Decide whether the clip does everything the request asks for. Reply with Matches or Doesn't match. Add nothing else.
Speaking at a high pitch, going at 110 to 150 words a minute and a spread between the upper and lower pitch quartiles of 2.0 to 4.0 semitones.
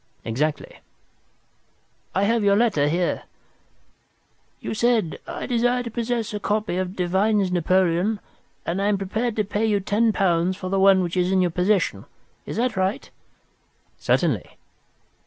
Matches